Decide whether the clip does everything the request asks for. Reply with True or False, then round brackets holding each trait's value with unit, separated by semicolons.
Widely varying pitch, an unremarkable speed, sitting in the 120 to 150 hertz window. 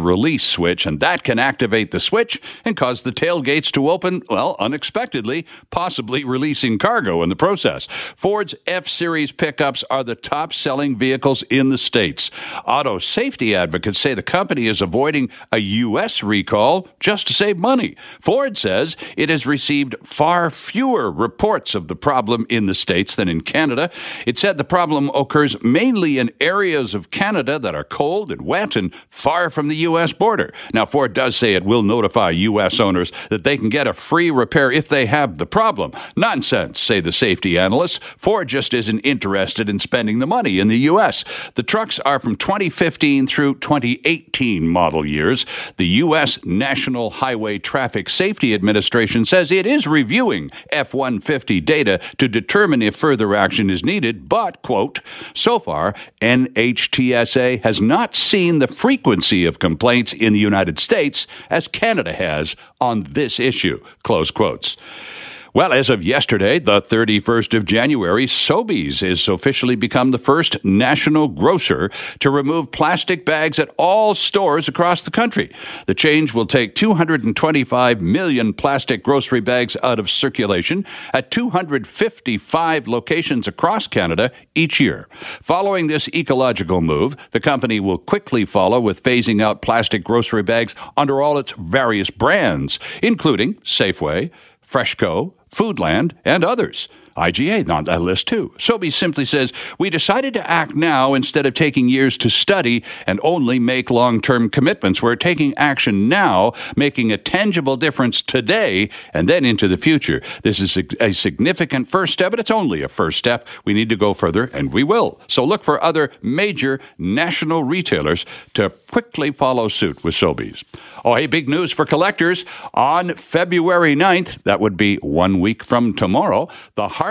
True (6.3 semitones; 160 wpm; 135 Hz)